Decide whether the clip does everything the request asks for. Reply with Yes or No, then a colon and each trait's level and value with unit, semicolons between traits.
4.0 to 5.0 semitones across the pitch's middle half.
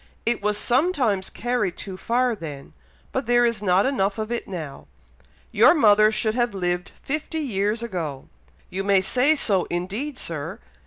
Yes: average, 4.5 semitones